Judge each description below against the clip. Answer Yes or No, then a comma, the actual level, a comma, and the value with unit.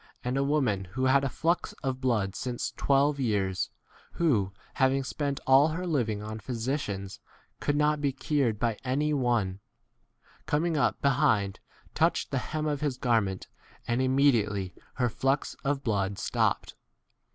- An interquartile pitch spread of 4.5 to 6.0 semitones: Yes, average, 4.9 semitones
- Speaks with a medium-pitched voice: No, low, 130 Hz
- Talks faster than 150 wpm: Yes, average, 160 wpm